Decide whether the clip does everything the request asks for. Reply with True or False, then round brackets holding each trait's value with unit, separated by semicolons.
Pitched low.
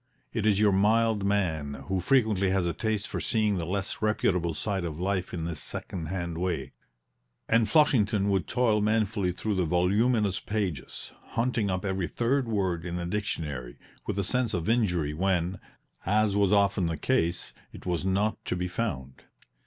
True (95 Hz)